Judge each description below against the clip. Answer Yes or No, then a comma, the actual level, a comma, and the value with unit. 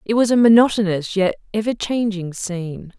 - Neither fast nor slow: Yes, average, 160 wpm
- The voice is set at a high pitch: Yes, high, 205 Hz